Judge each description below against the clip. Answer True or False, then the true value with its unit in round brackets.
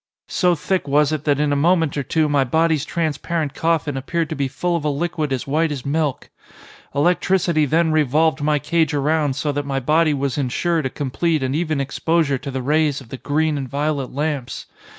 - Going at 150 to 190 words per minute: False (205 wpm)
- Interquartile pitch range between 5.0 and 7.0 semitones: False (2.5 semitones)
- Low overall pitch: False (150 Hz)